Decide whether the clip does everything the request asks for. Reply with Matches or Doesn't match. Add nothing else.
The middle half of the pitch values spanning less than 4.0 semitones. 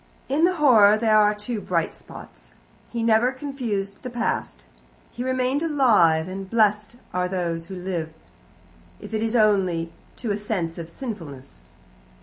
Doesn't match